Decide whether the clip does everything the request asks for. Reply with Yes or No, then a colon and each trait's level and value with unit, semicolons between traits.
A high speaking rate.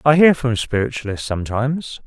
No: average, 145 wpm